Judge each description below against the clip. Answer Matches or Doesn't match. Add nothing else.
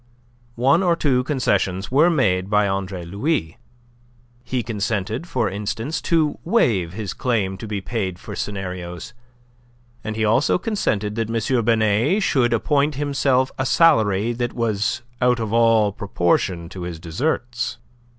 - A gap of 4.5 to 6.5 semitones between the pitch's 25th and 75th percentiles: Matches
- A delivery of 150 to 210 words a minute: Doesn't match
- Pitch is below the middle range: Matches